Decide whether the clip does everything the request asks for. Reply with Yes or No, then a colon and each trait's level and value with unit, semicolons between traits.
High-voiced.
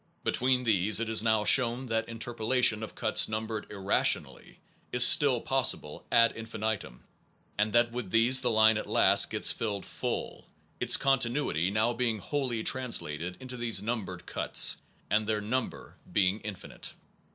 No: low, 110 Hz